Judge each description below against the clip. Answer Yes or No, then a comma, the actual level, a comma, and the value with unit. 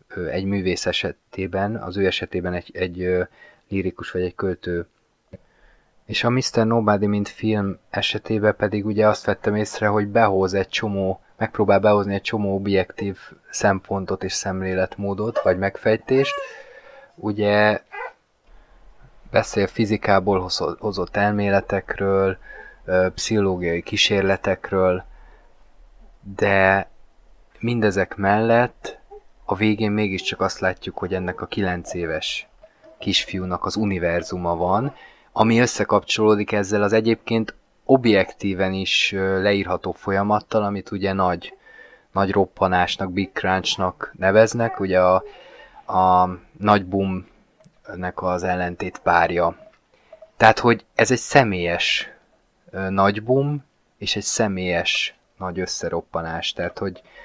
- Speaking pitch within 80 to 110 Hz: Yes, low, 100 Hz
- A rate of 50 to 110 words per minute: Yes, slow, 105 wpm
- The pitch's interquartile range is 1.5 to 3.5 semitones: Yes, narrow, 2.5 semitones